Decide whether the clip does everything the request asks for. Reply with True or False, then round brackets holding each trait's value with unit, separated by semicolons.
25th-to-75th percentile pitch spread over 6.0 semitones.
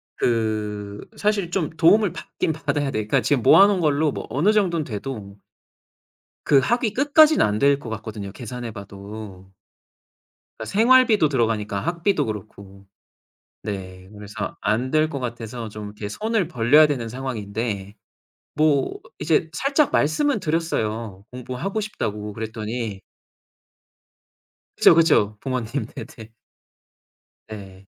True (7.3 semitones)